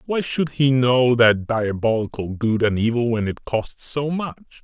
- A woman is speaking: No, male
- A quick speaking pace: No, average, 180 wpm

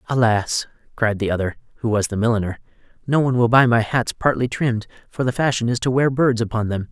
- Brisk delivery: Yes, fast, 215 wpm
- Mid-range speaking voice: No, low, 115 Hz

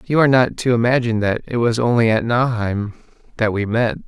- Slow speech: No, fast, 205 wpm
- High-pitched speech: No, low, 115 Hz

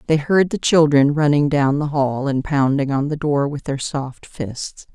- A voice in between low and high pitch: Yes, medium, 145 Hz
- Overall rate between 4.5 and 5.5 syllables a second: No, 4.2 syllables/s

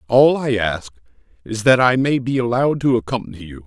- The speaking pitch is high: No, low, 120 Hz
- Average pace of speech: Yes, average, 195 wpm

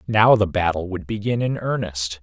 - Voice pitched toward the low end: Yes, low, 100 Hz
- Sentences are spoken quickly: No, average, 190 wpm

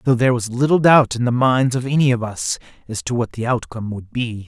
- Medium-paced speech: No, fast, 255 wpm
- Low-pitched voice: Yes, low, 125 Hz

